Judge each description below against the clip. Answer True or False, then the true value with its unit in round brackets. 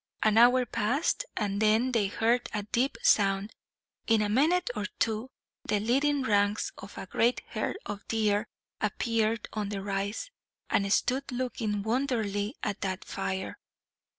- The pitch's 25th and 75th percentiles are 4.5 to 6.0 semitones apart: False (3.2 semitones)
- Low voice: False (220 Hz)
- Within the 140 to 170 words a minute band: True (150 wpm)